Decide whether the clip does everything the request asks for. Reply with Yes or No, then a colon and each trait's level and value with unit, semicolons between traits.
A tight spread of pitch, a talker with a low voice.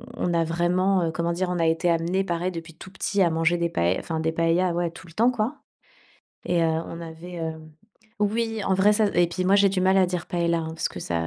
No: narrow, 2.3 semitones; medium, 175 Hz